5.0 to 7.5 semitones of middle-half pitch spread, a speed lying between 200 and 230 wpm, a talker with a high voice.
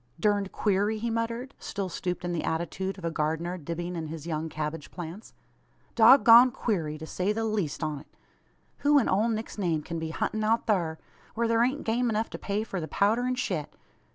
Yes: wide, 5.5 semitones; fast, 205 wpm; high, 195 Hz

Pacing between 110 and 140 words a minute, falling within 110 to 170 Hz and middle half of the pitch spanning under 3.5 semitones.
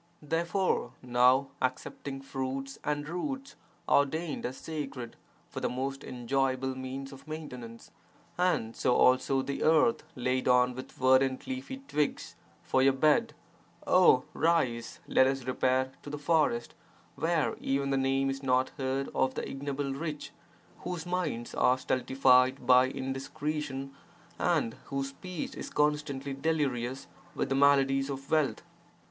Yes: slow, 135 wpm; low, 135 Hz; narrow, 2.5 semitones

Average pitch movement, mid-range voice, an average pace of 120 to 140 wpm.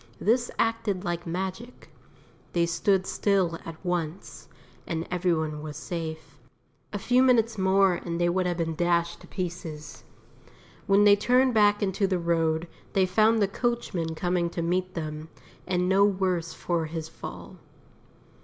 No: average, 3.1 semitones; medium, 180 Hz; average, 155 wpm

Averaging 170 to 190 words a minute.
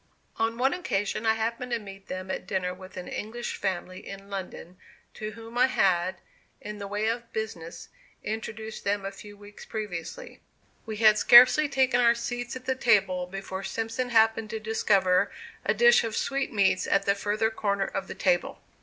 Yes: average, 180 wpm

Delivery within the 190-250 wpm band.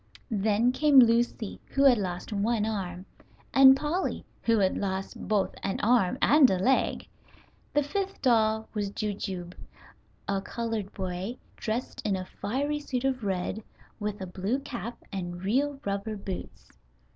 No: average, 145 wpm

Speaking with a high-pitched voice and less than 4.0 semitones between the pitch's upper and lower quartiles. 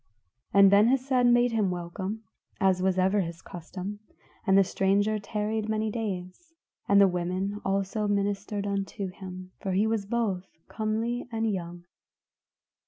Yes: high, 200 Hz; narrow, 2.6 semitones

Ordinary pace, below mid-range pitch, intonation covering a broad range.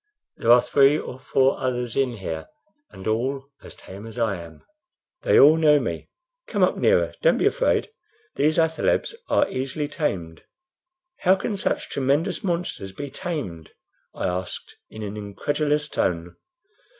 Yes: average, 150 wpm; low, 130 Hz; wide, 7.0 semitones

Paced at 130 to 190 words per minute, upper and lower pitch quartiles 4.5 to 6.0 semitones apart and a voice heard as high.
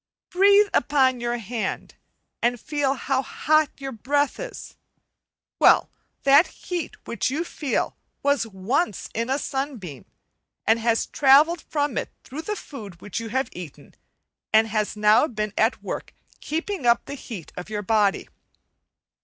Yes: average, 145 wpm; average, 4.8 semitones; very high, 260 Hz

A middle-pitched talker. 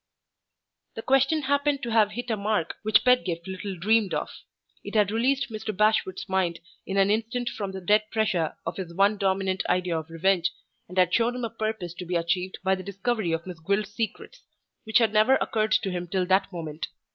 No: high, 200 Hz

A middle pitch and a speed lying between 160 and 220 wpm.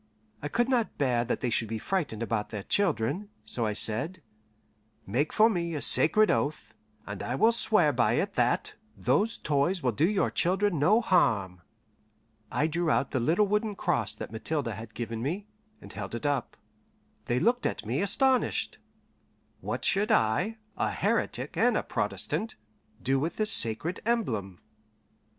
Yes: medium, 150 Hz; average, 165 wpm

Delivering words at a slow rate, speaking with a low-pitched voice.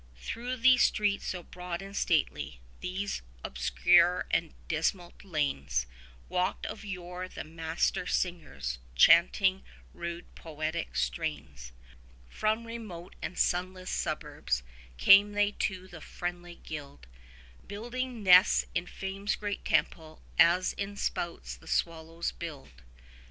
No: slow, 120 wpm; medium, 175 Hz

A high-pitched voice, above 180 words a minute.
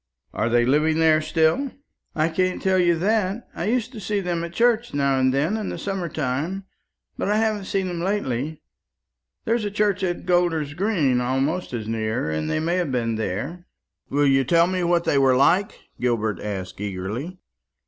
No: medium, 165 Hz; average, 190 wpm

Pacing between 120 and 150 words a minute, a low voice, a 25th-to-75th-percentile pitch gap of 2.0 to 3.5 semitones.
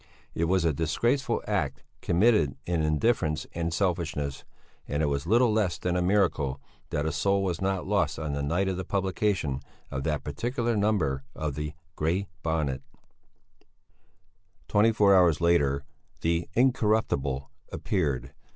No: average, 145 wpm; very low, 85 Hz; average, 4.9 semitones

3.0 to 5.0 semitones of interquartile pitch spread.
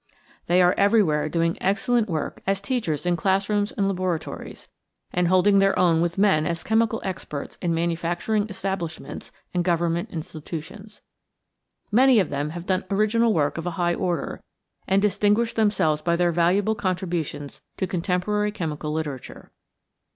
Yes: average, 3.5 semitones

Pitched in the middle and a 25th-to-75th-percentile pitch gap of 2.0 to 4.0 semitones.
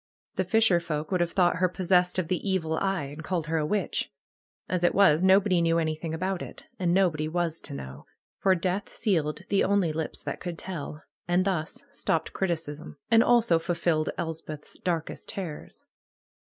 Yes: medium, 175 Hz; average, 2.9 semitones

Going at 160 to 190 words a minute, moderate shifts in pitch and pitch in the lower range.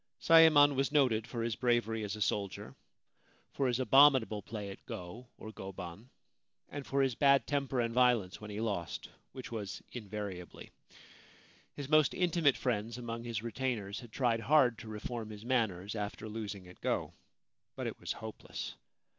Yes: average, 165 wpm; average, 3.9 semitones; low, 115 Hz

